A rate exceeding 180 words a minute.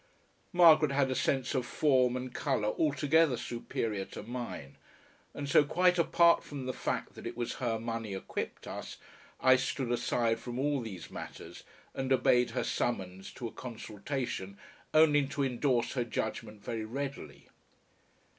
No: average, 155 wpm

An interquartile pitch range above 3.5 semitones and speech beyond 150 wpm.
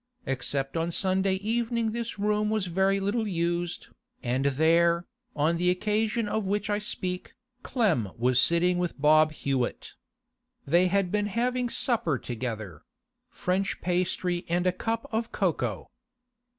No: average, 4.5 semitones; slow, 135 wpm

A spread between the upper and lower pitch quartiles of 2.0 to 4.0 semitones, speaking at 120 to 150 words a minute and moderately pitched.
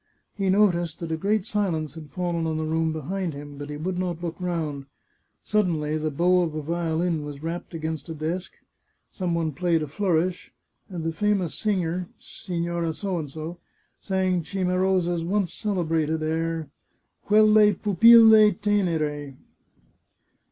Yes: average, 2.9 semitones; average, 145 wpm; medium, 170 Hz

